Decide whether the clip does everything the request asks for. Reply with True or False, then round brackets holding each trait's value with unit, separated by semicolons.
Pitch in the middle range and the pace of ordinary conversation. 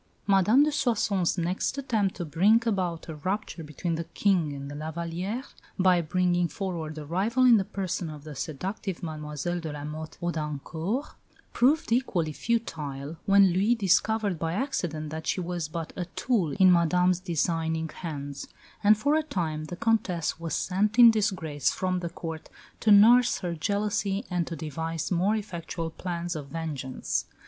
True (175 Hz; 165 wpm)